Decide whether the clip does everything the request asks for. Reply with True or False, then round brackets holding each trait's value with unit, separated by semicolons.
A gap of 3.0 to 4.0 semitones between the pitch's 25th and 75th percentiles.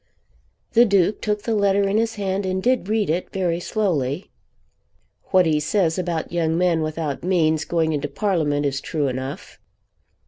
False (4.4 semitones)